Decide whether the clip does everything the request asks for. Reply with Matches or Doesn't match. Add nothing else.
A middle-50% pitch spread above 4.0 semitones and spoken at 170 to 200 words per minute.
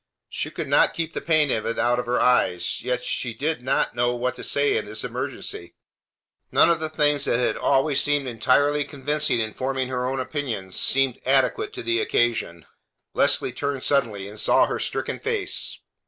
Doesn't match